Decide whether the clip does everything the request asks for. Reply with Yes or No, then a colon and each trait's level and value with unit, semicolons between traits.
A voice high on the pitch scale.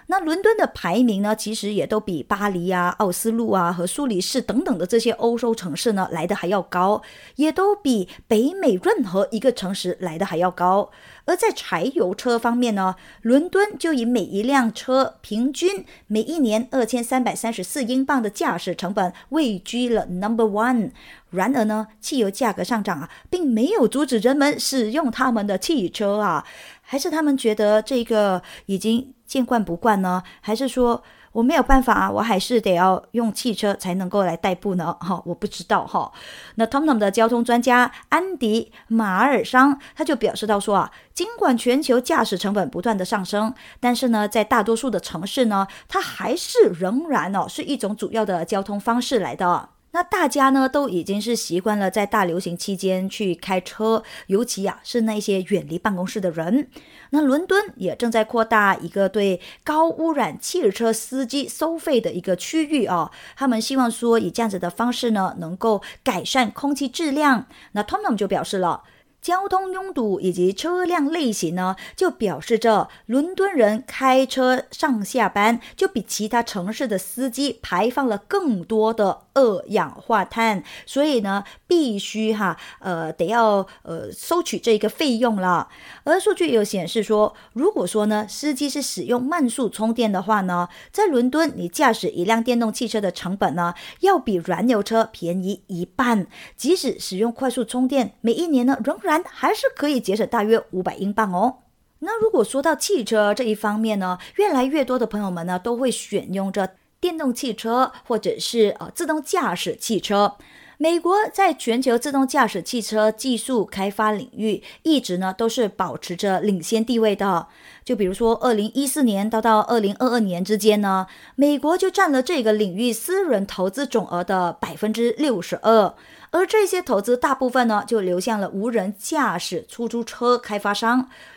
Yes: high, 230 Hz